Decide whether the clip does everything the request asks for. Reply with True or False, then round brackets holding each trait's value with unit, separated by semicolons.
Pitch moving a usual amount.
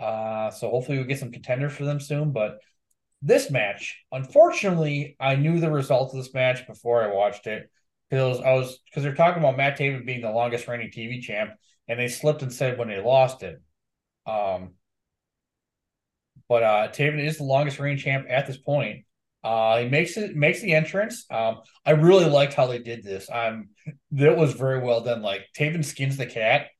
True (3.7 semitones)